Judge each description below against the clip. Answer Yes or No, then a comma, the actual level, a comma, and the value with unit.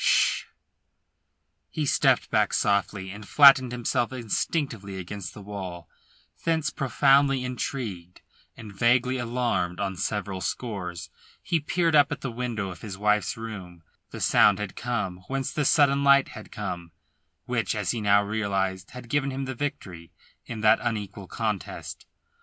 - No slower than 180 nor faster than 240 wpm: No, average, 150 wpm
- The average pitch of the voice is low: Yes, low, 110 Hz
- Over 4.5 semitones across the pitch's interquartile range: Yes, average, 5.2 semitones